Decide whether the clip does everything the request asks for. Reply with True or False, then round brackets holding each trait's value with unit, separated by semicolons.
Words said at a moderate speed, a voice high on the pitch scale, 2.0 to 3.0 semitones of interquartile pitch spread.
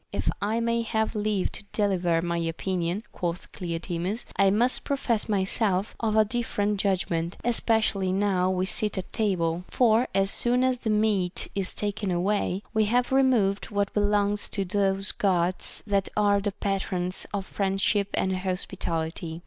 True (155 wpm; 200 Hz; 2.7 semitones)